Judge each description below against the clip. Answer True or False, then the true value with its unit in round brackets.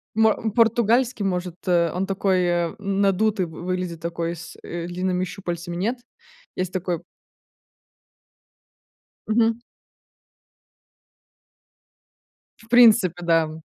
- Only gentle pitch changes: False (3.7 semitones)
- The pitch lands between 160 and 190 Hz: True (185 Hz)